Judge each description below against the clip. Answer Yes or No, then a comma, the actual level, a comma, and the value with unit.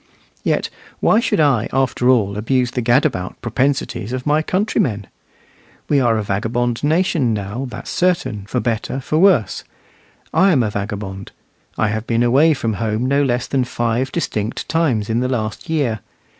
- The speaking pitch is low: Yes, low, 120 Hz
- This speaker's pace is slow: No, average, 165 wpm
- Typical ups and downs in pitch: Yes, average, 4.4 semitones